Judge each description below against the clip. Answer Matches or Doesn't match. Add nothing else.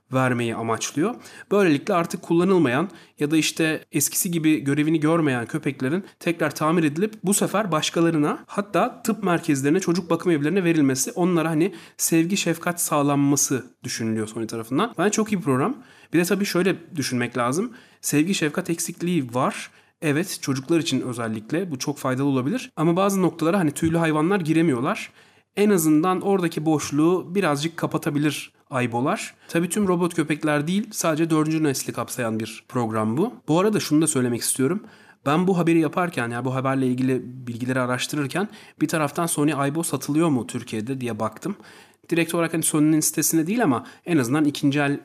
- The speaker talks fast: Matches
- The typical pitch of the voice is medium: Matches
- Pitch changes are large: Doesn't match